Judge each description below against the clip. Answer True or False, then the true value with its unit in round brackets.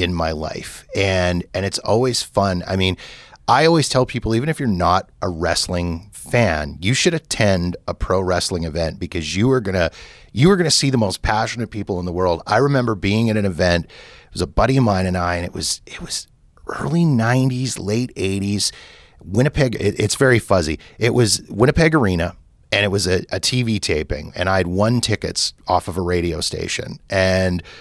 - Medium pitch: False (100 Hz)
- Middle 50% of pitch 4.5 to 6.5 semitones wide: True (5.1 semitones)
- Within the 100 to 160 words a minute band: False (200 wpm)